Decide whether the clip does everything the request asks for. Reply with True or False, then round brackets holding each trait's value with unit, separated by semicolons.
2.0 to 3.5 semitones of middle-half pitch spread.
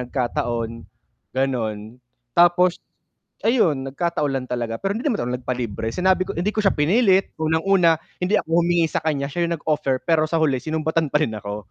False (5.6 semitones)